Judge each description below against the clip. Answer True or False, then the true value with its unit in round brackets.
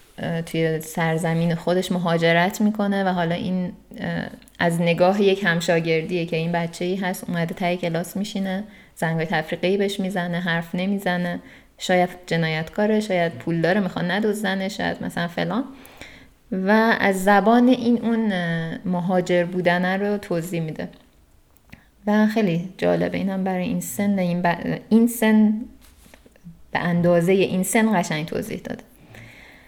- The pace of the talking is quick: False (135 wpm)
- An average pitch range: True (3.3 semitones)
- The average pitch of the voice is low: False (180 Hz)